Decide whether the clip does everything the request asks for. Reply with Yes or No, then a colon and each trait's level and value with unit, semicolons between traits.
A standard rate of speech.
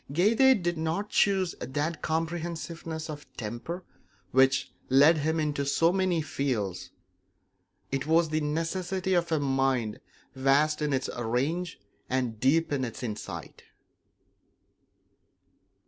No: slow, 115 wpm